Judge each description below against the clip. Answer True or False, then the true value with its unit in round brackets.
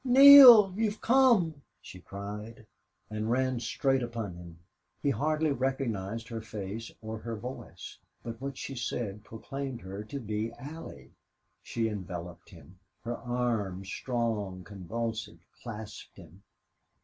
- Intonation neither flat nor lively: True (4.6 semitones)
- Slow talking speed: True (125 wpm)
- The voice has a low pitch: True (115 Hz)